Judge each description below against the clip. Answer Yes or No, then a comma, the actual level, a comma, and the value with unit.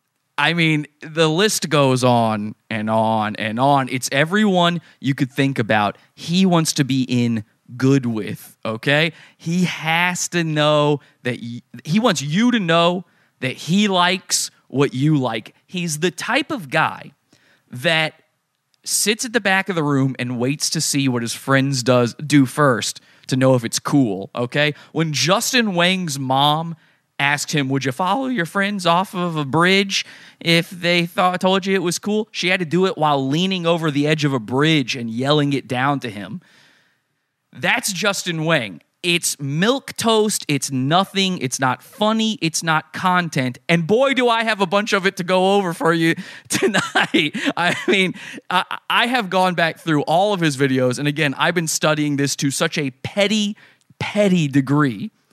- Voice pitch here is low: No, medium, 155 Hz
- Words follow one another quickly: No, average, 180 wpm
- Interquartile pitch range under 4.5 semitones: No, average, 5.1 semitones